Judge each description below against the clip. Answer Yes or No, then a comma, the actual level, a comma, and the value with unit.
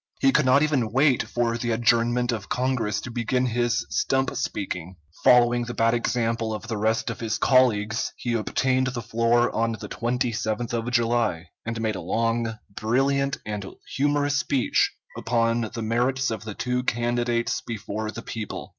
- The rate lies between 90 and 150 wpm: No, average, 165 wpm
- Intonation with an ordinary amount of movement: No, narrow, 1.8 semitones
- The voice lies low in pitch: Yes, low, 120 Hz